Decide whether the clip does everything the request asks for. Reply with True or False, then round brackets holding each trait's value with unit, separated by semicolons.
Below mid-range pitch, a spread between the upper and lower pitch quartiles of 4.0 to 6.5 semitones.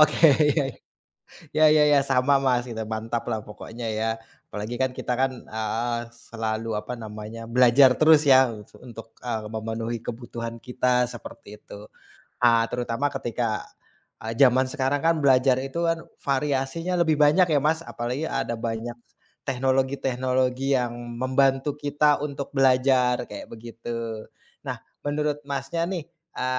False (125 Hz; 3.3 semitones)